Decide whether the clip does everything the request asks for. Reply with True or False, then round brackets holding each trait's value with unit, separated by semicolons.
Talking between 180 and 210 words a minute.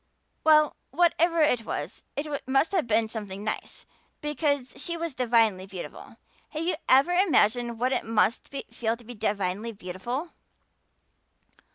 False (145 wpm)